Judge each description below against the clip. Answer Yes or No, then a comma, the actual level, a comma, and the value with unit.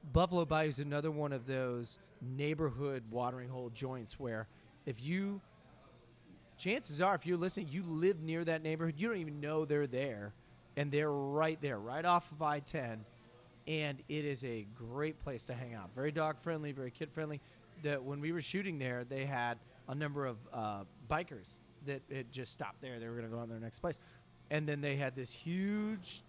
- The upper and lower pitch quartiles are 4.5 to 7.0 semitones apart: No, average, 4.0 semitones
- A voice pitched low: No, medium, 145 Hz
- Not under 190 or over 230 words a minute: Yes, average, 200 wpm